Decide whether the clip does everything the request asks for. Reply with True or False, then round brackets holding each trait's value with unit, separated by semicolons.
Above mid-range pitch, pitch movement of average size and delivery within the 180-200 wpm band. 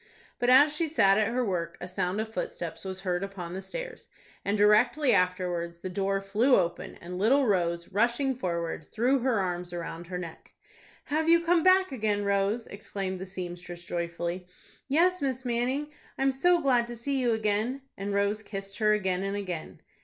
False (205 Hz; 5.8 semitones; 185 wpm)